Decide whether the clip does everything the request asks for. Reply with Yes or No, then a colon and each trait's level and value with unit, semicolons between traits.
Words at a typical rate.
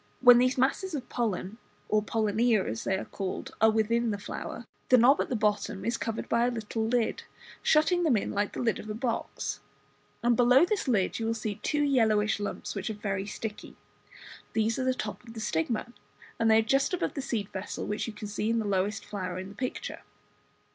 No: fast, 220 wpm